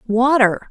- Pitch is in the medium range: No, high, 235 Hz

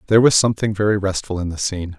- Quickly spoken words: Yes, fast, 240 wpm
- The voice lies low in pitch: Yes, low, 100 Hz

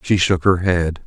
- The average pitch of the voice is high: No, very low, 90 Hz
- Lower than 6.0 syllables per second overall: Yes, 4.1 syllables/s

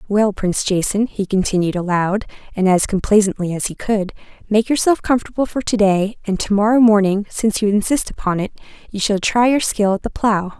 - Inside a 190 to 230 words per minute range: Yes, average, 200 wpm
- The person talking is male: No, female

